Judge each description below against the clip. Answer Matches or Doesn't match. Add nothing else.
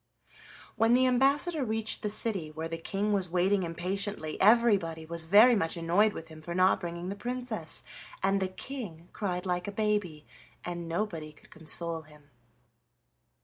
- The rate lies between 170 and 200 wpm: Doesn't match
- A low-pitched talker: Doesn't match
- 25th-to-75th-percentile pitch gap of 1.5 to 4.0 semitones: Doesn't match